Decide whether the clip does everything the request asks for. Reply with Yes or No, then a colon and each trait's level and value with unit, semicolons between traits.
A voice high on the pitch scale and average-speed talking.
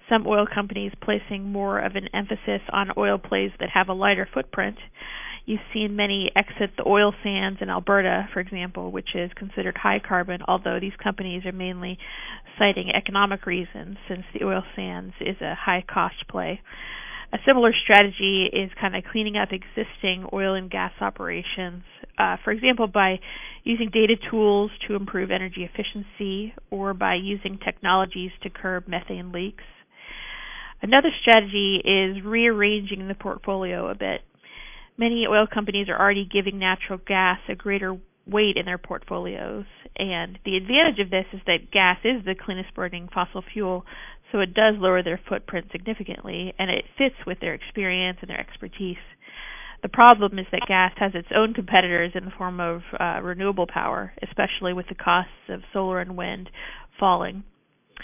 Yes: high, 195 Hz; average, 165 wpm